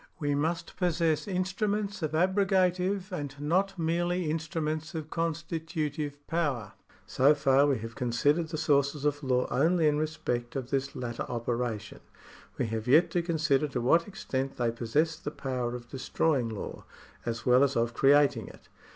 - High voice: No, medium, 150 Hz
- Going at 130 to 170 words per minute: Yes, average, 160 wpm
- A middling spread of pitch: Yes, average, 4.5 semitones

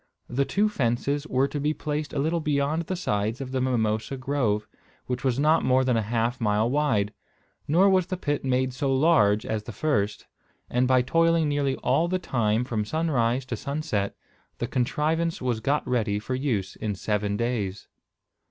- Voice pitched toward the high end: No, low, 130 Hz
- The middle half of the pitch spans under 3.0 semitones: No, average, 5.0 semitones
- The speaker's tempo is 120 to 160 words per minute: No, average, 180 wpm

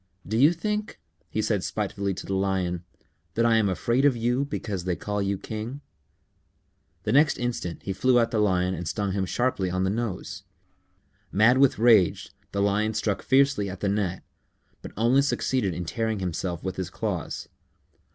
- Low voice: Yes, low, 105 Hz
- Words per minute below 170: No, average, 180 wpm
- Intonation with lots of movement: No, average, 4.3 semitones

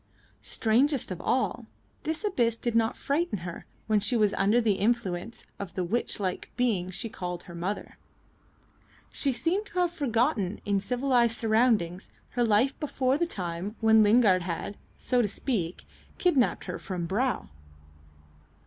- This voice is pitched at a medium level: No, high, 225 Hz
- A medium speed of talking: Yes, average, 150 wpm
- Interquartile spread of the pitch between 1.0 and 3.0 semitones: No, average, 4.7 semitones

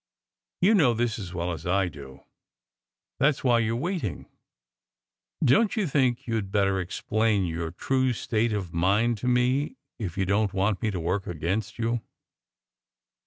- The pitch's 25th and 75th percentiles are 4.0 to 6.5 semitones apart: Yes, average, 4.8 semitones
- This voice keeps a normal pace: Yes, average, 175 wpm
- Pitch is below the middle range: Yes, low, 110 Hz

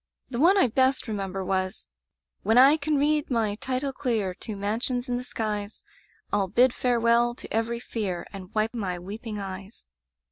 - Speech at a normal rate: Yes, average, 170 wpm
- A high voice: Yes, high, 225 Hz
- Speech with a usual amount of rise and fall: Yes, average, 3.9 semitones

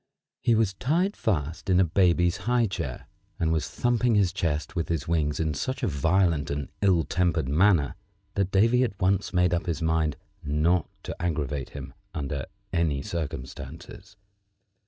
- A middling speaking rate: Yes, average, 160 wpm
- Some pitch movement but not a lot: Yes, average, 4.4 semitones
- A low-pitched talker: Yes, very low, 85 Hz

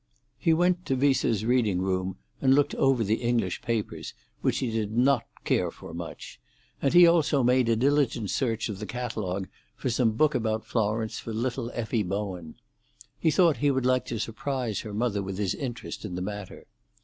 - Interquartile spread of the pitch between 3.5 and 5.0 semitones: Yes, average, 4.0 semitones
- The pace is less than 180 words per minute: No, average, 185 wpm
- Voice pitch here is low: Yes, low, 115 Hz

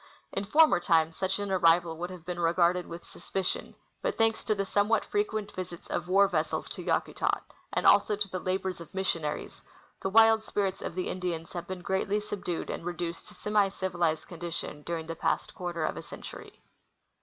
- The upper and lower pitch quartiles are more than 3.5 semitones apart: No, average, 2.8 semitones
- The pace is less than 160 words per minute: No, average, 190 wpm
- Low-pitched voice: No, medium, 185 Hz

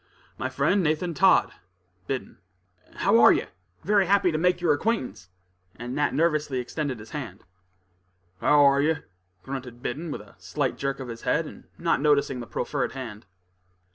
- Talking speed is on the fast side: No, average, 160 wpm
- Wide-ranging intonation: No, average, 4.3 semitones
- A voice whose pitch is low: No, medium, 145 Hz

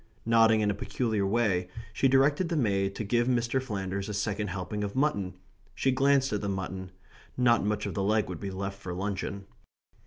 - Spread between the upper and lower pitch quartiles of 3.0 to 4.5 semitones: Yes, average, 3.5 semitones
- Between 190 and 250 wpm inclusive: Yes, average, 195 wpm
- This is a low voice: Yes, low, 105 Hz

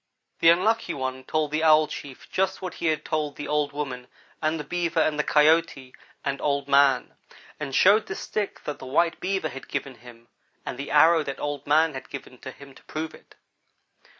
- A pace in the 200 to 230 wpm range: Yes, fast, 205 wpm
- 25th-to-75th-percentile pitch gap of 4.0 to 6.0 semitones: No, average, 3.0 semitones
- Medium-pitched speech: Yes, medium, 150 Hz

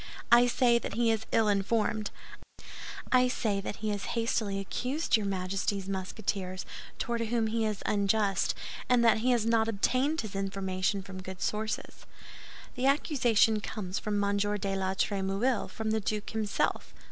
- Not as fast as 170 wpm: Yes, average, 160 wpm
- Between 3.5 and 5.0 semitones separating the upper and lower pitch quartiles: No, average, 2.8 semitones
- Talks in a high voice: Yes, high, 215 Hz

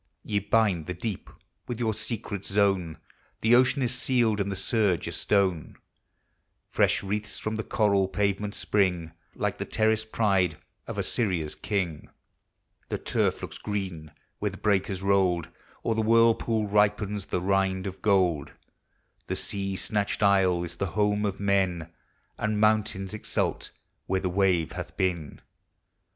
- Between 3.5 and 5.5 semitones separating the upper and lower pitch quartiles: No, narrow, 2.6 semitones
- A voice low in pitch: Yes, low, 100 Hz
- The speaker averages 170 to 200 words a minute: No, average, 150 wpm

